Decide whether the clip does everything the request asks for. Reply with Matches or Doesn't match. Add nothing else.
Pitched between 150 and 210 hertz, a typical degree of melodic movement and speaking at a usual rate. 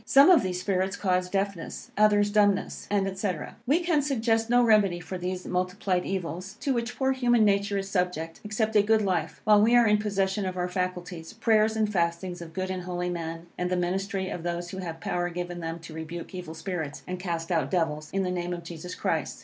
Doesn't match